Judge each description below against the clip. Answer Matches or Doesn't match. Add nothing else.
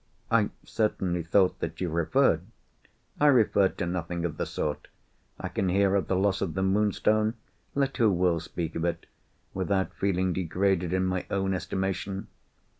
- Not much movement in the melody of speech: Matches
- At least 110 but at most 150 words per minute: Doesn't match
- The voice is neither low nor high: Doesn't match